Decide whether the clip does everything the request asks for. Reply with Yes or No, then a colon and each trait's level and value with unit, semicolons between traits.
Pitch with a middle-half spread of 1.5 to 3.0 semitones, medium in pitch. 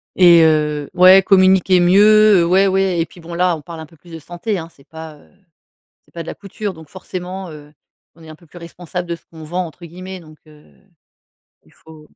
Yes: narrow, 2.6 semitones; medium, 170 Hz